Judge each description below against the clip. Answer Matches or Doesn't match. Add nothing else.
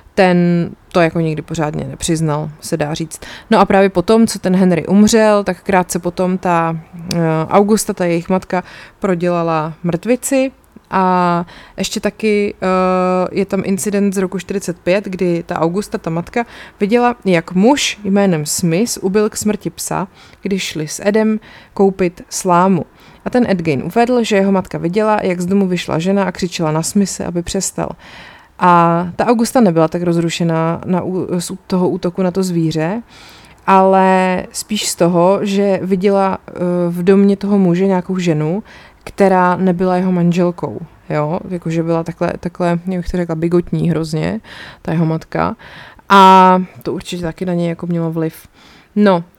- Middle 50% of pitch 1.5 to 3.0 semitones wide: Matches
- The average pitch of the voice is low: Doesn't match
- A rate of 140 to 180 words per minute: Matches